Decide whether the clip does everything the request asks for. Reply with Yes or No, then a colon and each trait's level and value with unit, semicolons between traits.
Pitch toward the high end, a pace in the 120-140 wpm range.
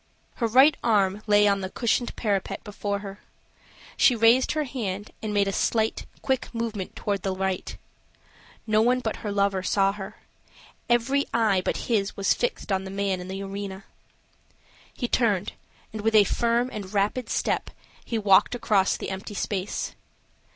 No: high, 205 Hz; average, 165 wpm